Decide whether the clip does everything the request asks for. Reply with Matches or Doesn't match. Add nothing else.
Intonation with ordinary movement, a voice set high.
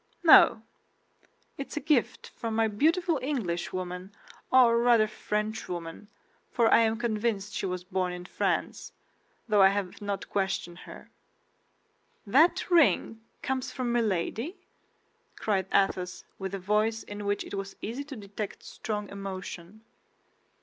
Matches